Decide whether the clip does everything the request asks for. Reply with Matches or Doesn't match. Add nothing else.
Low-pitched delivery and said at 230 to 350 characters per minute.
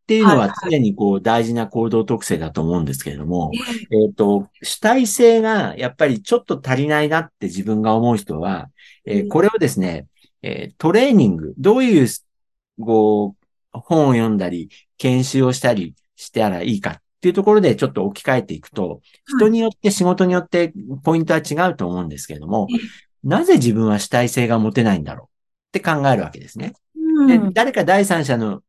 Doesn't match